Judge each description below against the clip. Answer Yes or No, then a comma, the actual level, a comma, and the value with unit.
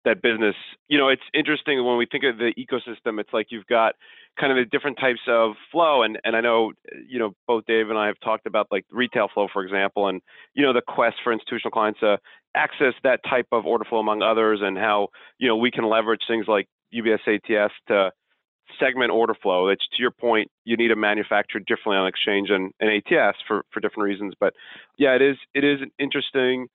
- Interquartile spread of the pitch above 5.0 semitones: No, average, 3.4 semitones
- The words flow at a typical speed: No, fast, 220 wpm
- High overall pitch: No, low, 115 Hz